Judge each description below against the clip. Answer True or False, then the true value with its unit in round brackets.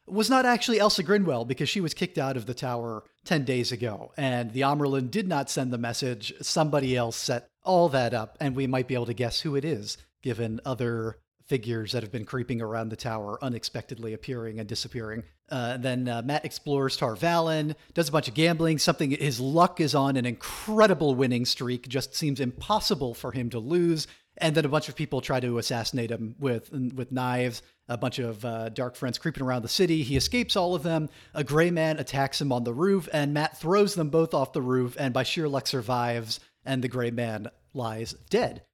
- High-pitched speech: False (135 Hz)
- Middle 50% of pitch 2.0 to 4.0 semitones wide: False (4.4 semitones)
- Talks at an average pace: False (210 wpm)